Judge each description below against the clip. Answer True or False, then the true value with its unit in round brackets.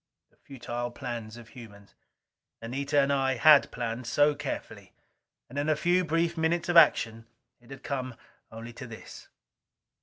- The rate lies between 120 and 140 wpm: False (155 wpm)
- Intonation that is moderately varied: True (4.1 semitones)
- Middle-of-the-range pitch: False (130 Hz)